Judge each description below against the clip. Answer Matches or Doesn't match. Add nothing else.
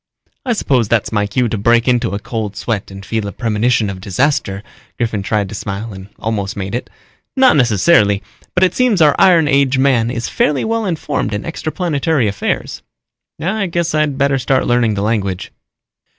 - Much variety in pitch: Matches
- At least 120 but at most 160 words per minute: Doesn't match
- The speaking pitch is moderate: Doesn't match